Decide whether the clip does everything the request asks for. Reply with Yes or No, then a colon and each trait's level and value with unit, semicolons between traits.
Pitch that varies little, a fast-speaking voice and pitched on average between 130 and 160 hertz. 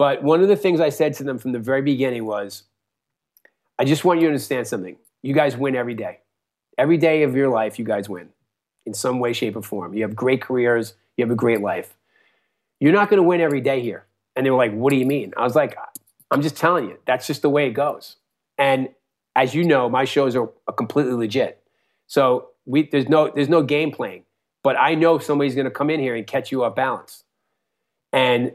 No: average, 3.4 semitones; fast, 230 wpm; low, 135 Hz